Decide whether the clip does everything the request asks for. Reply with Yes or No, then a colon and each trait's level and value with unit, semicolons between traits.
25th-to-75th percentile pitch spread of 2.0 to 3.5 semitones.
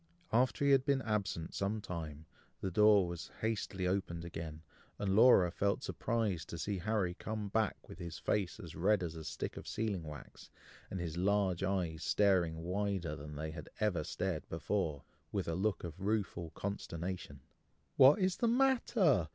No: average, 4.2 semitones